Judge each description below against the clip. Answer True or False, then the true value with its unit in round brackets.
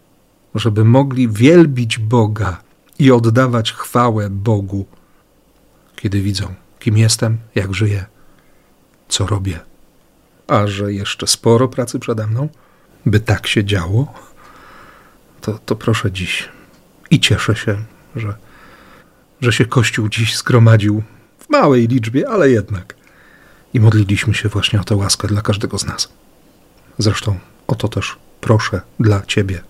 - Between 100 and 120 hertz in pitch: True (110 Hz)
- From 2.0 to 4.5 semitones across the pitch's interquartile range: True (2.9 semitones)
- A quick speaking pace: False (125 wpm)